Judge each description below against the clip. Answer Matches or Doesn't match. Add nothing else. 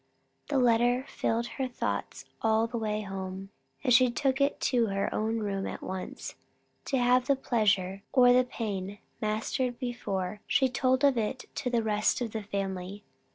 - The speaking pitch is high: Matches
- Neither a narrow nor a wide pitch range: Matches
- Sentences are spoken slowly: Doesn't match